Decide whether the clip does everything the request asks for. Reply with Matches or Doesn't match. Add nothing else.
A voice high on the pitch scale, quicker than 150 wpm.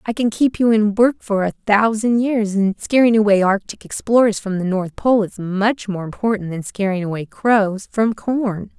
Matches